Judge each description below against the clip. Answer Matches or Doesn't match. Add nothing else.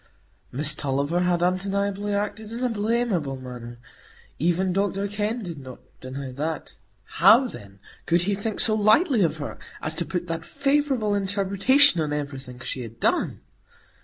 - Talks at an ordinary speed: Matches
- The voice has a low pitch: Doesn't match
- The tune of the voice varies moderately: Doesn't match